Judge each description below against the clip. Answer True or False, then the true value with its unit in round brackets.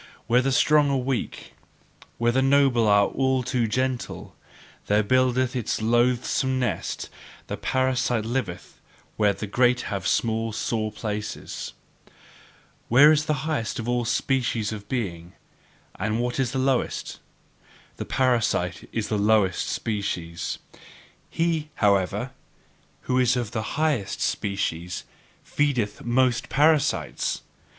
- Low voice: True (120 Hz)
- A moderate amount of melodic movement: True (3.6 semitones)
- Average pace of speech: False (125 wpm)